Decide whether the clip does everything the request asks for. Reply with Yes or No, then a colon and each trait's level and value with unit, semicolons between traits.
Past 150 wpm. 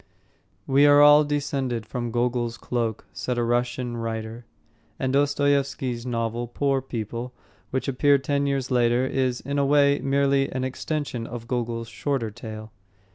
No: average, 145 wpm